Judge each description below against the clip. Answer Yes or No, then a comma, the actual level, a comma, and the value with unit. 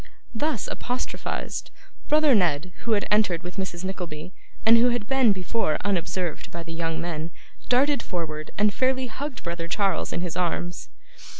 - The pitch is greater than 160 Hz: Yes, high, 190 Hz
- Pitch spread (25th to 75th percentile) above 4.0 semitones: Yes, wide, 5.6 semitones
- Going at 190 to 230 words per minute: No, average, 160 wpm